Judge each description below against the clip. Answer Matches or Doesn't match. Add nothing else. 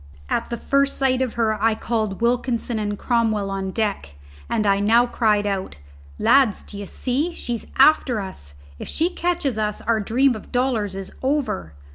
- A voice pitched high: Matches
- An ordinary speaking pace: Matches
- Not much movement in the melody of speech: Doesn't match